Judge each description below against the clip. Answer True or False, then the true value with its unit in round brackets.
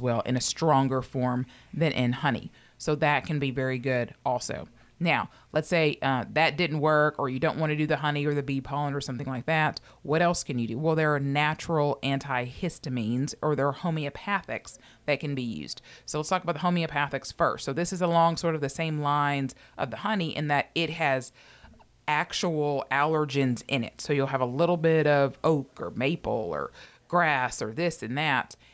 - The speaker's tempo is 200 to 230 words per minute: True (205 wpm)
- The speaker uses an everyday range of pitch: True (3.2 semitones)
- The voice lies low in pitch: False (145 Hz)